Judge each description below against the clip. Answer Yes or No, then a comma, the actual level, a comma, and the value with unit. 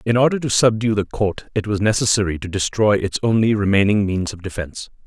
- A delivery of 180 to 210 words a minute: Yes, average, 200 wpm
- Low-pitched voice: Yes, low, 105 Hz